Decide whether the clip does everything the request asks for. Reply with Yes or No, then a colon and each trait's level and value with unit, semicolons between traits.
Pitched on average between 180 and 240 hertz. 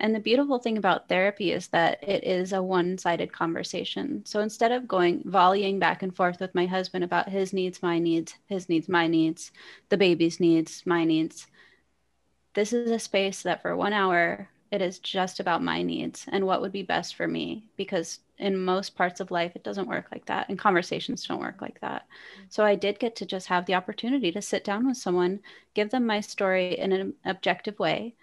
Yes: high, 190 Hz